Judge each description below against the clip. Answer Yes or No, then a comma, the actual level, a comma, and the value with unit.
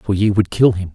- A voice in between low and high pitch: No, low, 100 Hz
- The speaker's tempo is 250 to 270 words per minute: No, fast, 315 wpm